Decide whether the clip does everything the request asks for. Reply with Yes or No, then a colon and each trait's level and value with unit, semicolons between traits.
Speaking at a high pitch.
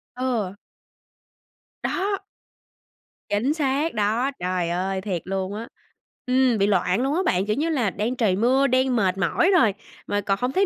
Yes: high, 225 Hz